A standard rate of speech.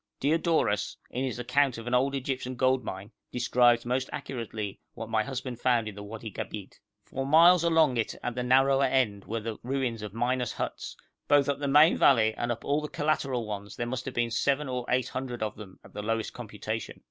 No: fast, 210 wpm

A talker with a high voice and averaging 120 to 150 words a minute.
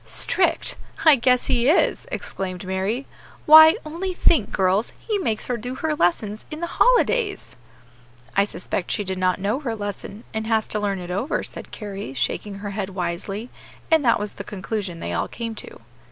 No: high, 210 Hz; average, 180 wpm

